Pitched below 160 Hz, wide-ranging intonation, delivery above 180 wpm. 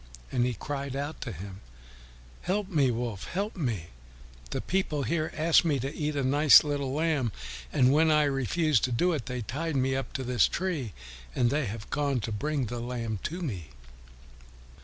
No: medium, 140 Hz; average, 4.2 semitones; average, 190 wpm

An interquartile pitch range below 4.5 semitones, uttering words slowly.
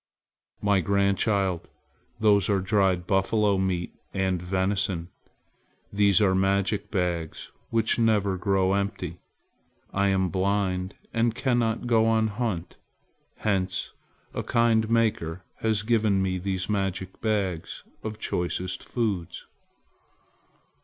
Yes: narrow, 2.6 semitones; slow, 110 wpm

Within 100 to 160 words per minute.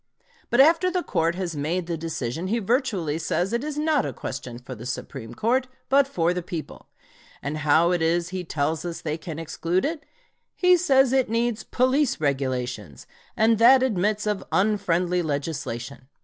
No: average, 175 wpm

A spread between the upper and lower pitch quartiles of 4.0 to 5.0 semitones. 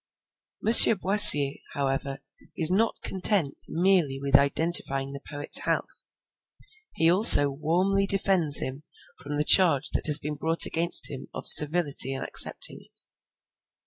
Yes: average, 4.6 semitones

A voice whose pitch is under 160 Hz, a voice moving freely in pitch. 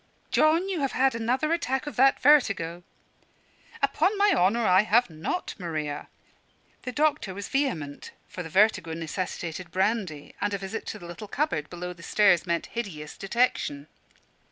No: high, 200 Hz; wide, 7.5 semitones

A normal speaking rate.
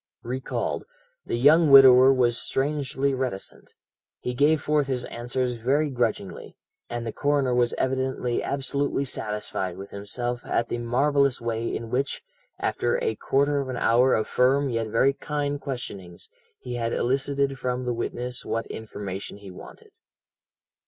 Yes: average, 145 wpm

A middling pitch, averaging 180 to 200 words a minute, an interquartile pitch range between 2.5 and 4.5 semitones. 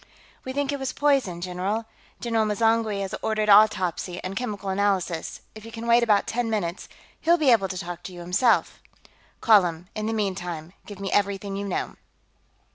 No: high, 205 Hz; average, 185 wpm; average, 3.5 semitones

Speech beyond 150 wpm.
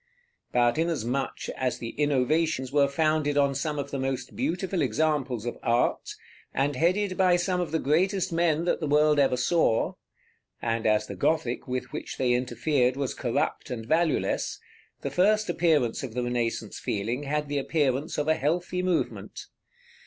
Yes: average, 165 wpm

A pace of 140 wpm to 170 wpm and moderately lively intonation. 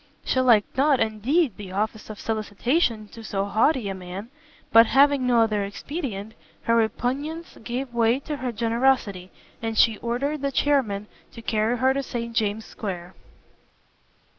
Yes: average, 155 wpm; average, 3.8 semitones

